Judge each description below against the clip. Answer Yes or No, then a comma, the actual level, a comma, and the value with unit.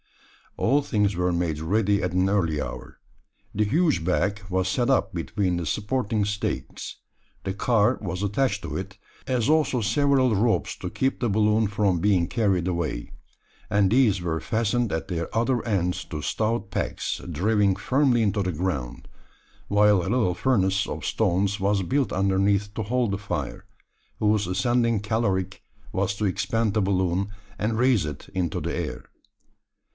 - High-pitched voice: No, low, 100 Hz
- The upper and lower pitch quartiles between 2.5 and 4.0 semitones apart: Yes, average, 3.5 semitones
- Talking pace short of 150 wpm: No, average, 160 wpm